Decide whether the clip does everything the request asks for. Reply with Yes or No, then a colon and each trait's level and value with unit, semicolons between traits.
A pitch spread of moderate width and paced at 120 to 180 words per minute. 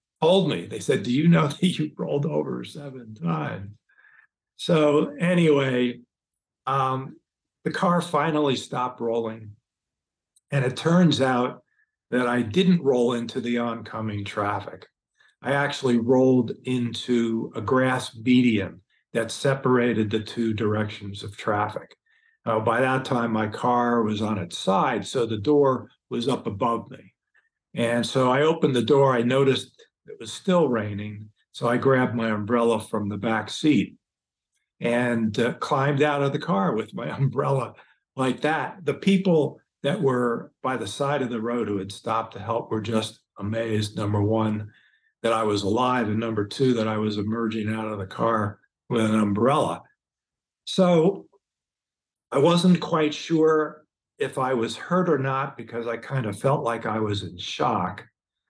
Yes: average, 4.3 semitones; average, 160 wpm